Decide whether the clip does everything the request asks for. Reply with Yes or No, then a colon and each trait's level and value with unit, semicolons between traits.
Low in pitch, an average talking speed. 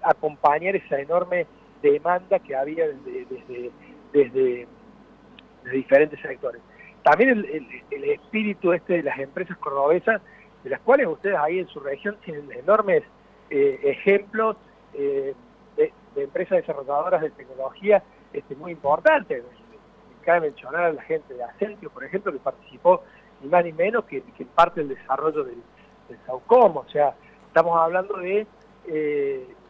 No: high, 195 Hz; average, 150 wpm